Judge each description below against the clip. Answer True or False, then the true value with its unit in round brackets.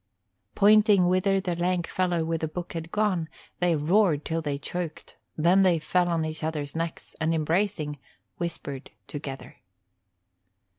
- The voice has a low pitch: False (170 Hz)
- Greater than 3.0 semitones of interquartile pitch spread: False (2.6 semitones)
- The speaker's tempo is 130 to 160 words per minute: True (145 wpm)